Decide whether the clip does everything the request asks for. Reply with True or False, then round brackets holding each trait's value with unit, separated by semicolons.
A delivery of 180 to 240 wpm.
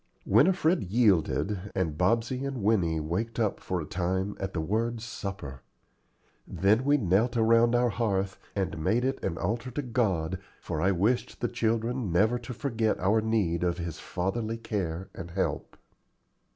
False (160 wpm)